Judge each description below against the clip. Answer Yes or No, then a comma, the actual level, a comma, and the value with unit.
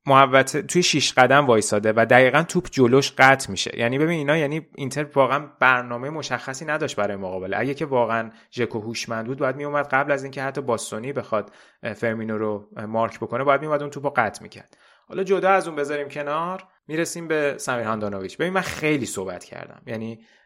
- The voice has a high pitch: No, low, 135 Hz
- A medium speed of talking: No, fast, 185 wpm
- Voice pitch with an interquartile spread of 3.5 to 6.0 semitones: Yes, average, 4.5 semitones